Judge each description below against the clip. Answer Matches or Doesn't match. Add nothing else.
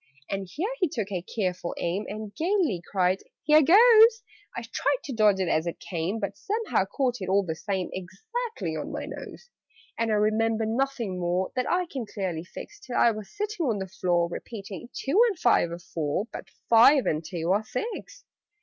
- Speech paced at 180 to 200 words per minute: Matches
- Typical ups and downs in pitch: Doesn't match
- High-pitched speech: Matches